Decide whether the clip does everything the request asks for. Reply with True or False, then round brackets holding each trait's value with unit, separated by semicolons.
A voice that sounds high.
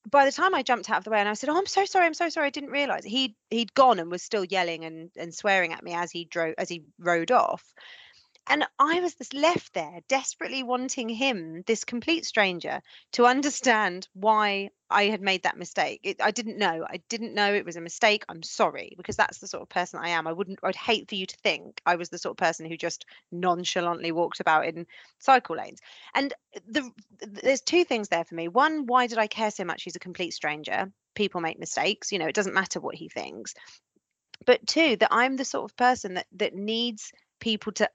True (210 Hz)